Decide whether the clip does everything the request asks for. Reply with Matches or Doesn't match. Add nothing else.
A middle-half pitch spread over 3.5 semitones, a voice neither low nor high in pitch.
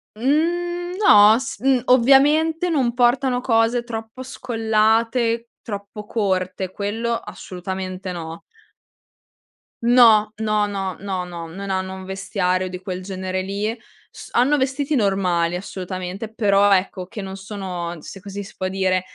Doesn't match